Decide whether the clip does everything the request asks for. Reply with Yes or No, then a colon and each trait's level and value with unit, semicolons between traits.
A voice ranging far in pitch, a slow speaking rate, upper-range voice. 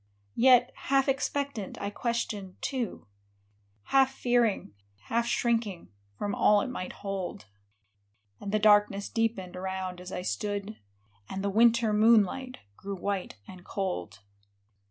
No: average, 3.7 semitones; slow, 125 wpm; high, 205 Hz